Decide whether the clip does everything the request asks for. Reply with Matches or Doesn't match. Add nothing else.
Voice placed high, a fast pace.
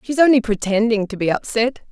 Doesn't match